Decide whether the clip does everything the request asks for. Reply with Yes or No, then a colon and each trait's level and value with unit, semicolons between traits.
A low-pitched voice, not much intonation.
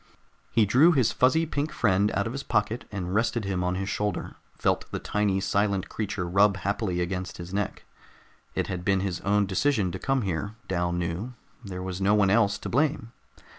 No: low, 100 Hz; average, 3.3 semitones